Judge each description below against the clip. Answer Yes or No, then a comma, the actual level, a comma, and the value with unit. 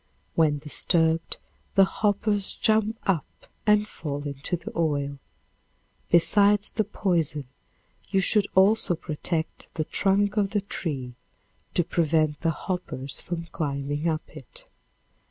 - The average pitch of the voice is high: No, medium, 170 Hz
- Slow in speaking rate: Yes, slow, 120 wpm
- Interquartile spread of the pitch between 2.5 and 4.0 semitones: No, average, 5.1 semitones